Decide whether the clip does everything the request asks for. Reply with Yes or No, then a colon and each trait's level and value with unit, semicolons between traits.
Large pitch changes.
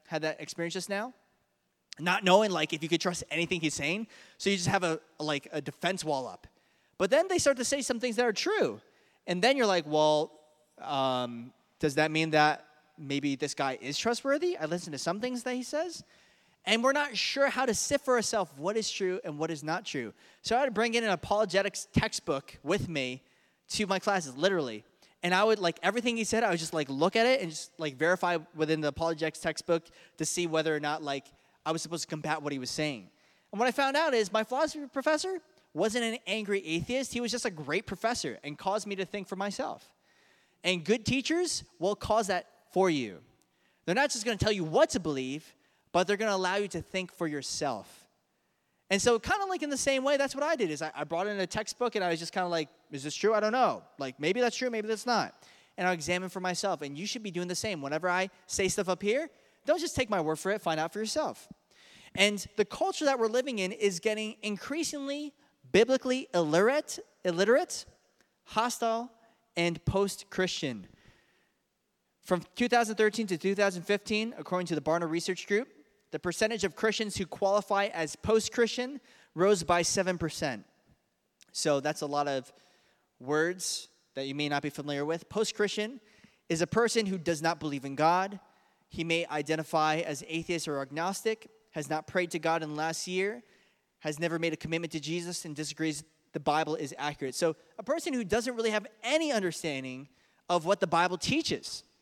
Yes: wide, 6.0 semitones